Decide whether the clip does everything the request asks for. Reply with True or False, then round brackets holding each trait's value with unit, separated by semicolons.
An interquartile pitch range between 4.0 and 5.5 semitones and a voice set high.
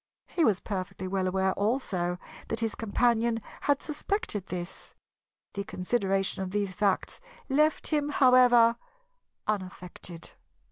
True (4.5 semitones; 205 Hz)